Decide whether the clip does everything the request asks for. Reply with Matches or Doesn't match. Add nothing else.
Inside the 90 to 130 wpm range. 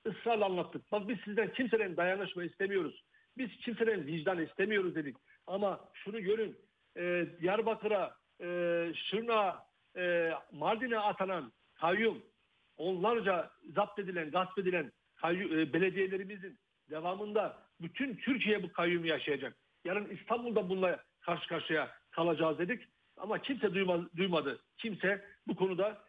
Matches